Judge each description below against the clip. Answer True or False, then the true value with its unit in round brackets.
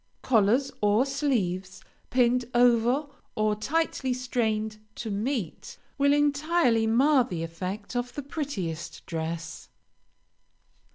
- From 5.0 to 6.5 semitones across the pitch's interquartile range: True (5.3 semitones)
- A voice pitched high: True (235 Hz)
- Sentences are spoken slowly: True (105 wpm)